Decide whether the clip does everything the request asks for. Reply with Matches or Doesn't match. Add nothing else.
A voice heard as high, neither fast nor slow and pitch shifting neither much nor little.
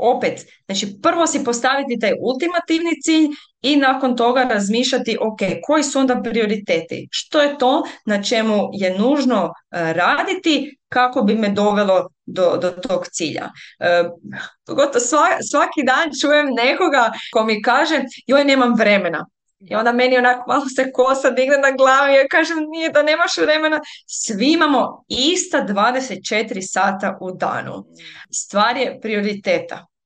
Doesn't match